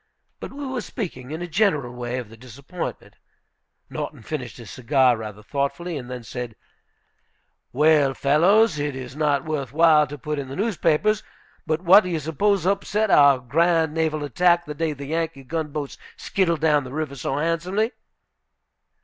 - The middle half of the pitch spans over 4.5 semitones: No, average, 4.2 semitones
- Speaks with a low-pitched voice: No, medium, 150 Hz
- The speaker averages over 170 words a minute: No, average, 165 wpm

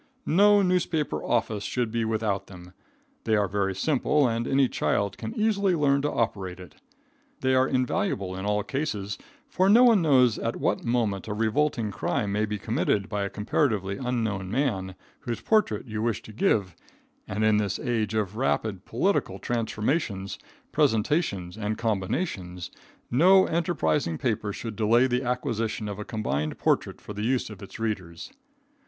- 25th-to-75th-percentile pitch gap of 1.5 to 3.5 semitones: No, average, 4.8 semitones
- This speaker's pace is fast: No, average, 160 wpm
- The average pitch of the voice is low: Yes, low, 110 Hz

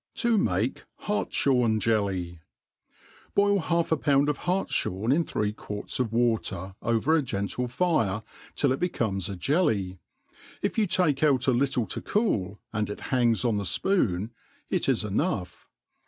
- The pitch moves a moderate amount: No, wide, 7.2 semitones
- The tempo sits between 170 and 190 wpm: No, average, 150 wpm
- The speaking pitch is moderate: No, low, 120 Hz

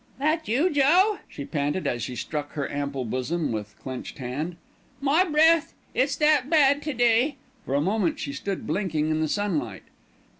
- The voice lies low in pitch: No, medium, 185 Hz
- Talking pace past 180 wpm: No, average, 175 wpm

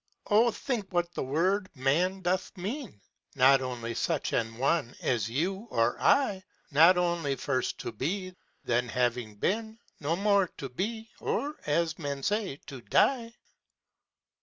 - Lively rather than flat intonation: Yes, wide, 7.4 semitones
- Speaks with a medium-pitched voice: Yes, medium, 170 Hz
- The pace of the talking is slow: No, average, 160 wpm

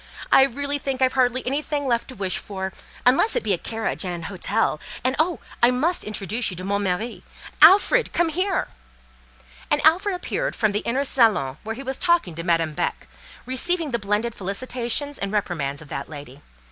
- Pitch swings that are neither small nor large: No, wide, 6.6 semitones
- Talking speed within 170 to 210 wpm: Yes, average, 185 wpm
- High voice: Yes, high, 235 Hz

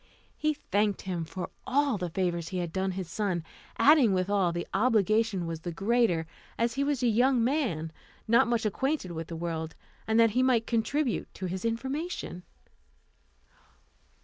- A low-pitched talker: No, high, 215 Hz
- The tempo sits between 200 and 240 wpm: No, average, 165 wpm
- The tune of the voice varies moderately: No, wide, 5.7 semitones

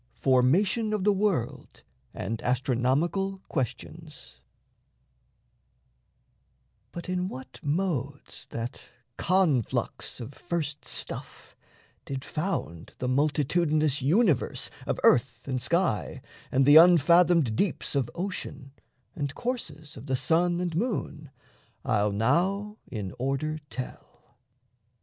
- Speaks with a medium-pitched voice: Yes, medium, 150 Hz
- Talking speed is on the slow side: Yes, slow, 105 wpm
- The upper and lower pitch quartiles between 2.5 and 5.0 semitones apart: No, wide, 5.6 semitones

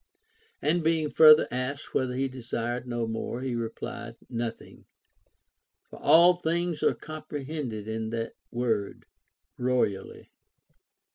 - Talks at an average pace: No, slow, 120 wpm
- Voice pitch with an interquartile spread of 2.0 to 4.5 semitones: No, average, 4.9 semitones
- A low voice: Yes, low, 125 Hz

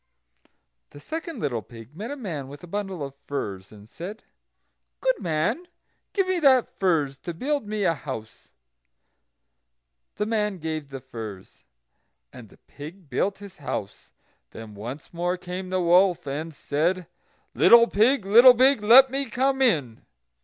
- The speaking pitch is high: No, medium, 180 Hz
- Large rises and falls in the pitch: Yes, wide, 8.2 semitones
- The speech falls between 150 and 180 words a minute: Yes, average, 155 wpm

